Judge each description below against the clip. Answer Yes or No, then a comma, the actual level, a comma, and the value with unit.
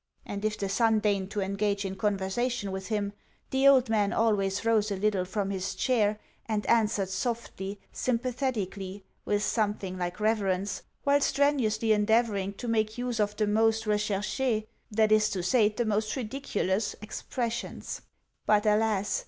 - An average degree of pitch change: No, narrow, 2.2 semitones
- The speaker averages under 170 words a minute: Yes, average, 155 wpm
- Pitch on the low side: No, high, 210 Hz